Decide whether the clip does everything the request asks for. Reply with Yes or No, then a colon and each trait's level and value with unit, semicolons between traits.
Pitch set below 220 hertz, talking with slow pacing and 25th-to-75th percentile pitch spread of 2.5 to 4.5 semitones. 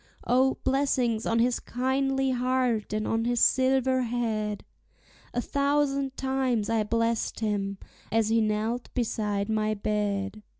No: high, 230 Hz; slow, 130 wpm; average, 3.4 semitones